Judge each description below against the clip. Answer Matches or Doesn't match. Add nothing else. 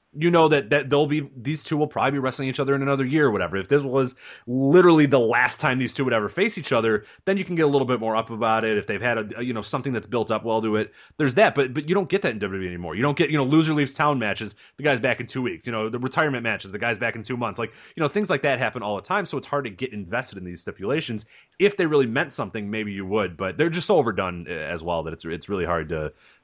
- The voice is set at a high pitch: Doesn't match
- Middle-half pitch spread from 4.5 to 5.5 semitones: Matches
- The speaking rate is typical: Doesn't match